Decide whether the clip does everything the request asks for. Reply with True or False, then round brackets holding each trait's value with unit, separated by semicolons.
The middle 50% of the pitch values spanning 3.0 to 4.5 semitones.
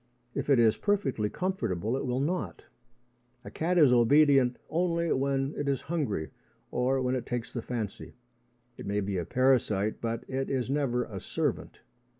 True (3.9 semitones)